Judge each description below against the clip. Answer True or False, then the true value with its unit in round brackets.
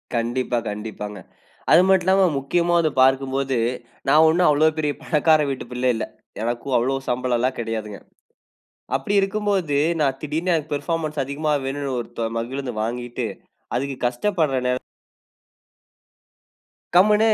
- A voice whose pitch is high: False (140 Hz)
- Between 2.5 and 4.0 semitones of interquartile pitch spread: False (4.4 semitones)